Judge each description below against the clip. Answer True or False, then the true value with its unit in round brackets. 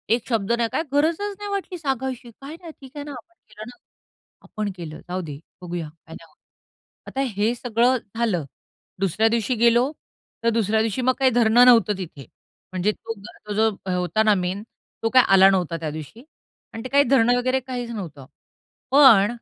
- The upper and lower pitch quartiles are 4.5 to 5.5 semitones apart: True (4.9 semitones)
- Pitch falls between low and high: False (225 Hz)